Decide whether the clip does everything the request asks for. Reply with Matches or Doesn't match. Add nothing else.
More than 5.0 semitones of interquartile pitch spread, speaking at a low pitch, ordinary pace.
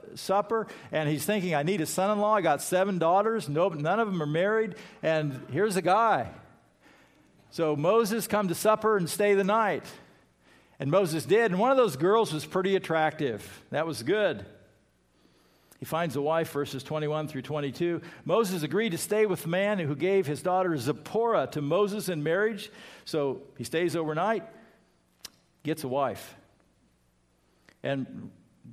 Doesn't match